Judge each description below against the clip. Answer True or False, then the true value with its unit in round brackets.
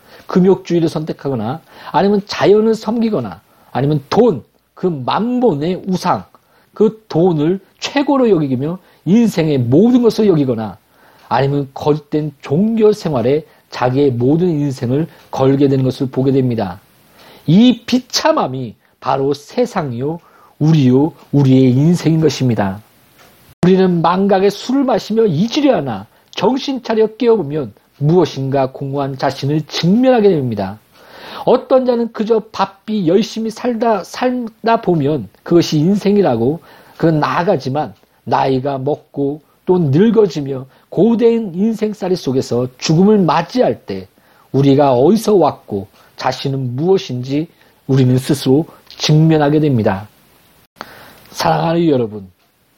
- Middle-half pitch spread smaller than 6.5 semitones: False (7.1 semitones)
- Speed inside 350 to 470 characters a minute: False (270 characters per minute)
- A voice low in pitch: False (160 Hz)